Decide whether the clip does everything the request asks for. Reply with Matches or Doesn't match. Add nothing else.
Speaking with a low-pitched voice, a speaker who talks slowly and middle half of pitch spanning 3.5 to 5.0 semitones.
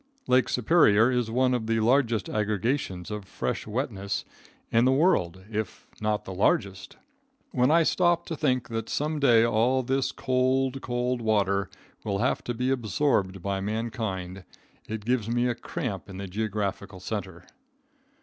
Doesn't match